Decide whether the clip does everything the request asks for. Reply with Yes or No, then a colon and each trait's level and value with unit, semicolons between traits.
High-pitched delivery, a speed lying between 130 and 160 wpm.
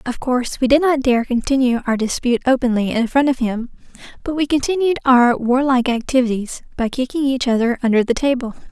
No: very high, 255 Hz; average, 195 wpm